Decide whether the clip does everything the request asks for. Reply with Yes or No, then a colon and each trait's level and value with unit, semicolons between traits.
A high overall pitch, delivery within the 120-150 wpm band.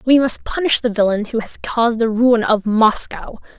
No: high, 230 Hz; average, 200 wpm